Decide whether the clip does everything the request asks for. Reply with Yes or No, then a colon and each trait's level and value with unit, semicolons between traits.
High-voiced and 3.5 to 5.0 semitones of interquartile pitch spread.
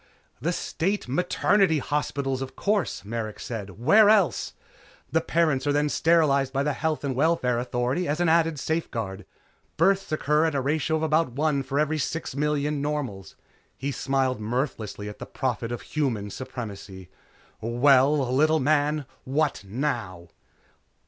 No: medium, 140 Hz; average, 4.1 semitones